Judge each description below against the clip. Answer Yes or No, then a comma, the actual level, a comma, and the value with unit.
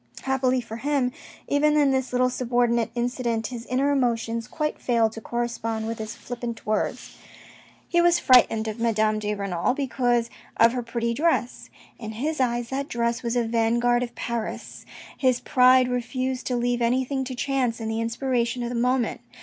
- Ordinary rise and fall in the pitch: No, narrow, 1.9 semitones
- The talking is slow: No, average, 175 wpm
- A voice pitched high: Yes, high, 240 Hz